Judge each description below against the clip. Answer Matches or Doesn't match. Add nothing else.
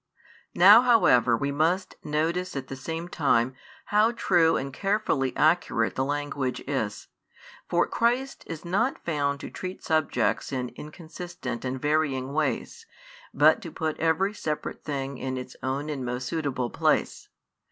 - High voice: Doesn't match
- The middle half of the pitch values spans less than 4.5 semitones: Doesn't match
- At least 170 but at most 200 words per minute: Doesn't match